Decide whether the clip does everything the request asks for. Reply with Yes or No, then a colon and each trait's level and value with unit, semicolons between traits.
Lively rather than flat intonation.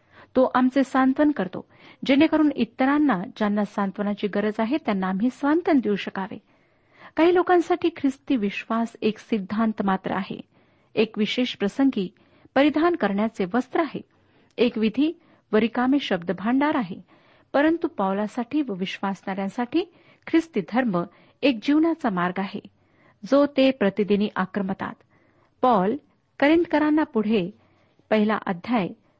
Yes: wide, 5.7 semitones